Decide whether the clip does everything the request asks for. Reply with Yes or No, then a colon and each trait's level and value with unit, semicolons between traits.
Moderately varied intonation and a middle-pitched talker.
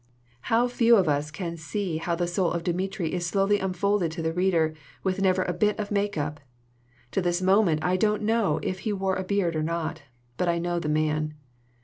Yes: average, 3.5 semitones; medium, 180 Hz